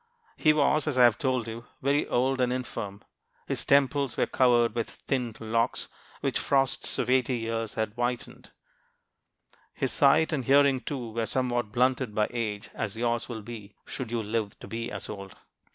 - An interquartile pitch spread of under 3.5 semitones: Yes, narrow, 2.6 semitones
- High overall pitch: No, low, 120 Hz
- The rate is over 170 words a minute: Yes, average, 185 wpm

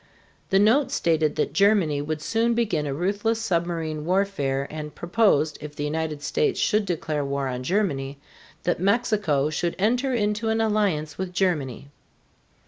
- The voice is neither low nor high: Yes, medium, 175 Hz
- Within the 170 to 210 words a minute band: No, average, 150 wpm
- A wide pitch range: Yes, wide, 5.9 semitones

